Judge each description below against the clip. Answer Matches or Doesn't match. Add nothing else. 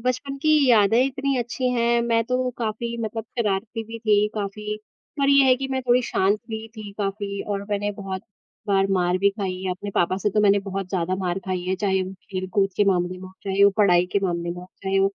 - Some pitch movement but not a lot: Matches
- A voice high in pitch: Matches